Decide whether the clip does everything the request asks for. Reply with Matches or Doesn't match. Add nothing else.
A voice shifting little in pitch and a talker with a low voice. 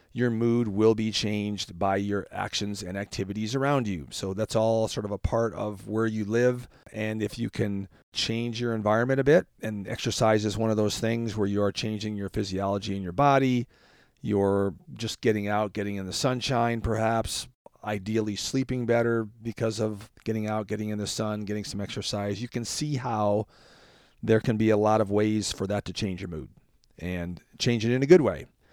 Matches